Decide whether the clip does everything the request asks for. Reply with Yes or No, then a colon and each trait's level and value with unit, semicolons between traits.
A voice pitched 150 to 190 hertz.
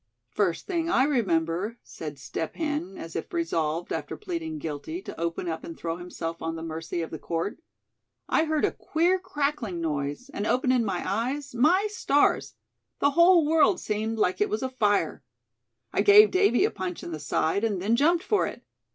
No: high, 220 Hz